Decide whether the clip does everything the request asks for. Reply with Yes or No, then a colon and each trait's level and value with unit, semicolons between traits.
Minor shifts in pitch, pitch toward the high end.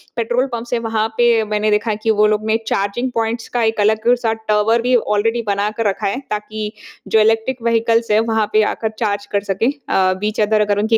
Yes: narrow, 1.6 semitones; high, 220 Hz